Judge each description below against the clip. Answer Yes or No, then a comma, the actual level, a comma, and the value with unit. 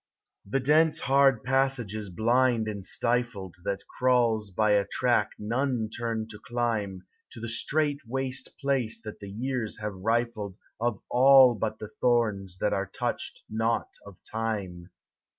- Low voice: Yes, low, 115 Hz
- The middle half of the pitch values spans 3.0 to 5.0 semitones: Yes, average, 3.4 semitones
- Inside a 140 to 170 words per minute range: Yes, average, 150 wpm